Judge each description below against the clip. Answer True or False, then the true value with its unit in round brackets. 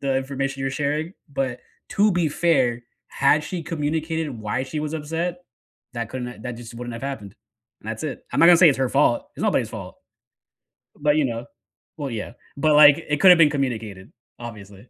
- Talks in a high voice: False (135 Hz)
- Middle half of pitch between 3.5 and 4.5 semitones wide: True (4.2 semitones)